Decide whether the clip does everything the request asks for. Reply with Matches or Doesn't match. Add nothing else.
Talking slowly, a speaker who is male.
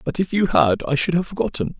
Doesn't match